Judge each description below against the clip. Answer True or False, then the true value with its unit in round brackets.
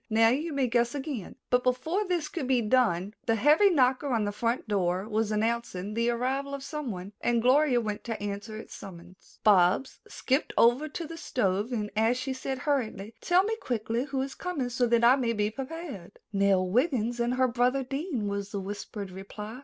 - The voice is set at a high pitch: True (240 Hz)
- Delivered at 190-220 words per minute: True (195 wpm)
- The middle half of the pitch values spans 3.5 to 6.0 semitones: True (4.4 semitones)